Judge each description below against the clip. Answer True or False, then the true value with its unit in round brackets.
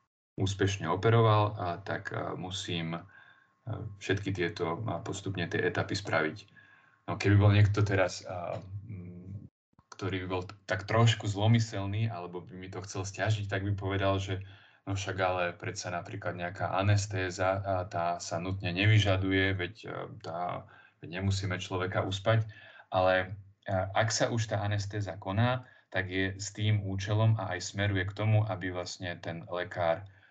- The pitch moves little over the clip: True (2.1 semitones)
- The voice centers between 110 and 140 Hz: False (95 Hz)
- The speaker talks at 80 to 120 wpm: False (145 wpm)